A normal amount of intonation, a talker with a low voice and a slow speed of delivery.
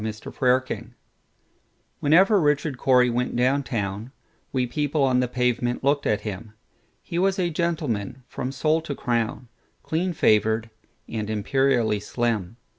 Yes: average, 4.5 semitones; low, 125 Hz; slow, 120 wpm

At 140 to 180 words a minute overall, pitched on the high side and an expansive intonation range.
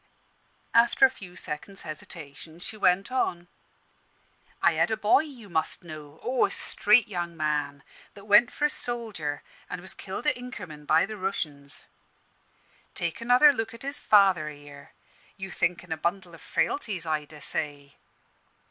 No: average, 155 wpm; medium, 180 Hz; wide, 6.3 semitones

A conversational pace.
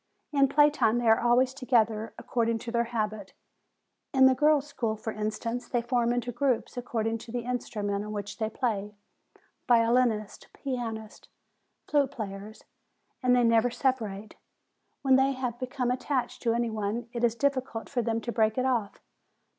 Yes: average, 170 wpm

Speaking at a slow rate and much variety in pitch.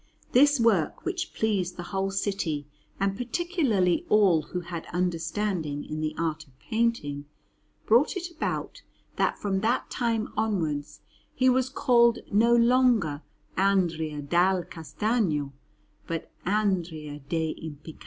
Yes: slow, 125 wpm; wide, 6.4 semitones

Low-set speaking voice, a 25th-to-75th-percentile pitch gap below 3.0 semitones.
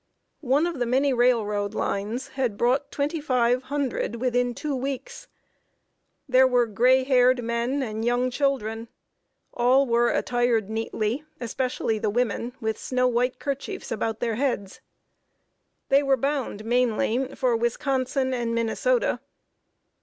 No: high, 245 Hz; narrow, 2.5 semitones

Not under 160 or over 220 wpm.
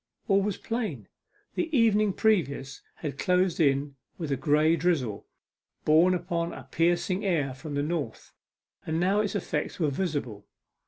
No: average, 150 wpm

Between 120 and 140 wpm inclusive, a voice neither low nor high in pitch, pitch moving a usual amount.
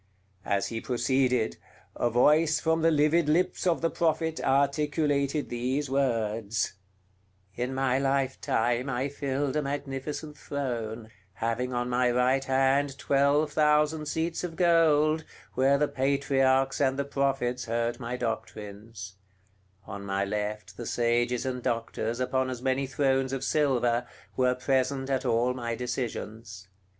No: slow, 135 wpm; low, 130 Hz; average, 3.0 semitones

